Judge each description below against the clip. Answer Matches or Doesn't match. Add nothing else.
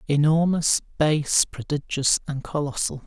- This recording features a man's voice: Matches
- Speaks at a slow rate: Matches